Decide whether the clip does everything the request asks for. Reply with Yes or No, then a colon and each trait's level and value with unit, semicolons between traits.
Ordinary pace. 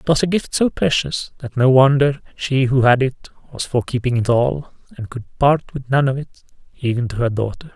No: fast, 215 wpm